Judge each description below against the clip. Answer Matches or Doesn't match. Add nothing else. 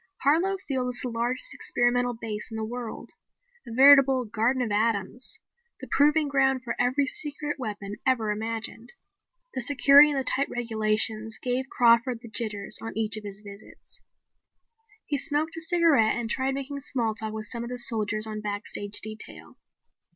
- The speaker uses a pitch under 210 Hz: Doesn't match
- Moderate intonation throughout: Matches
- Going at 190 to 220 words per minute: Doesn't match